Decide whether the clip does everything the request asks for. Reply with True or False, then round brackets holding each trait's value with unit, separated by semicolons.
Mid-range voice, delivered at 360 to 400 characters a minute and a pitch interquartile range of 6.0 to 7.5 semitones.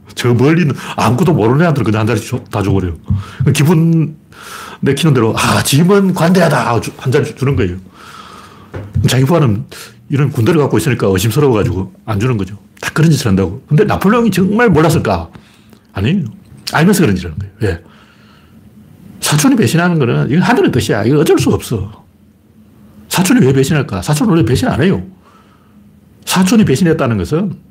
False (125 Hz; 365 characters per minute; 7.2 semitones)